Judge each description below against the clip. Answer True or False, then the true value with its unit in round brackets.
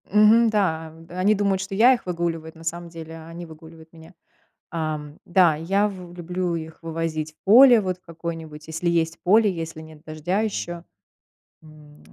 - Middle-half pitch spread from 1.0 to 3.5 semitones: True (2.8 semitones)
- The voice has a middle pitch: True (170 Hz)